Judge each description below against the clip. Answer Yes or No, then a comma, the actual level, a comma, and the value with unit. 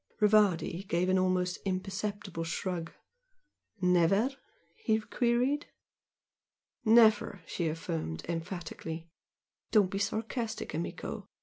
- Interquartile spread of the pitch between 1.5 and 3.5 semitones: No, average, 4.1 semitones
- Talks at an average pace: No, slow, 90 wpm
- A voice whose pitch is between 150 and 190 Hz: Yes, medium, 185 Hz